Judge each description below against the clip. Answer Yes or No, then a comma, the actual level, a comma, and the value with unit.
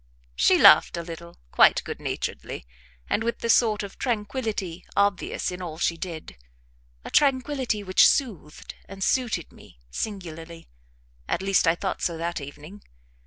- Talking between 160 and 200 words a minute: No, average, 150 wpm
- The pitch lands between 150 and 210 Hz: Yes, medium, 185 Hz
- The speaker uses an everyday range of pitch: Yes, average, 4.6 semitones